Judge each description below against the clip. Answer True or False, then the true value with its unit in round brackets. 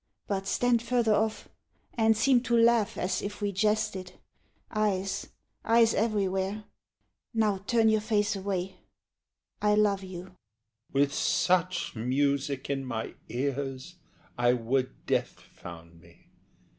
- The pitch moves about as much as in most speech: False (7.5 semitones)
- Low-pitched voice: False (195 Hz)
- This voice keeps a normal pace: False (125 wpm)